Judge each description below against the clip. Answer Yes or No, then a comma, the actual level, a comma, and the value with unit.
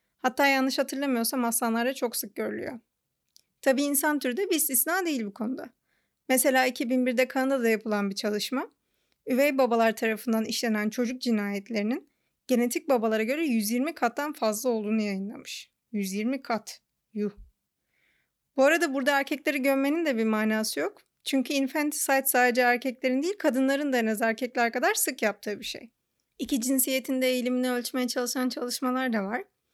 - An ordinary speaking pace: No, fast, 145 wpm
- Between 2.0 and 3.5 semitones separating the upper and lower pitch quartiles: Yes, average, 3.2 semitones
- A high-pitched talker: Yes, very high, 255 Hz